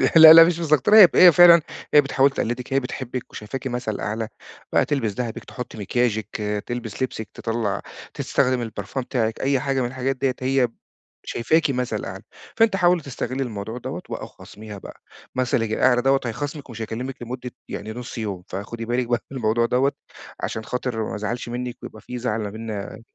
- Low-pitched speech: Yes, low, 125 Hz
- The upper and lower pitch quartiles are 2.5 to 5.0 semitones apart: Yes, average, 3.2 semitones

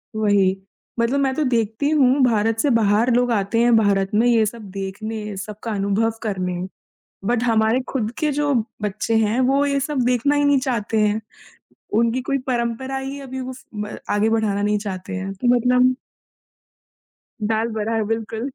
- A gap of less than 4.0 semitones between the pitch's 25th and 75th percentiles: Yes, average, 3.5 semitones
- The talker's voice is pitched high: Yes, high, 225 Hz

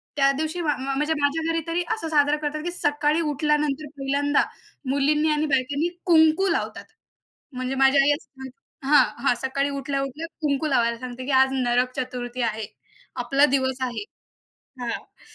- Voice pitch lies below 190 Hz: No, very high, 280 Hz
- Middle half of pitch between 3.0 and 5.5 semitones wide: No, narrow, 2.6 semitones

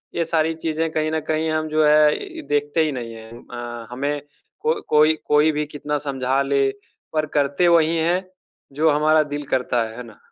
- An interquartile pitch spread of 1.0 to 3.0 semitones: Yes, narrow, 2.4 semitones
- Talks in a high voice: No, medium, 150 Hz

